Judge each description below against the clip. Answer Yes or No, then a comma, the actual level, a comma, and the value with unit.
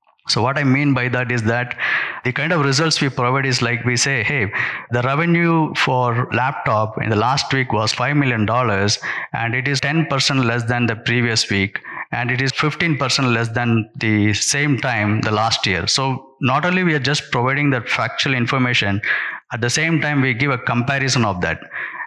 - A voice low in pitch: Yes, low, 125 Hz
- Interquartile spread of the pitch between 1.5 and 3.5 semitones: Yes, average, 3.1 semitones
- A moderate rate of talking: Yes, average, 195 wpm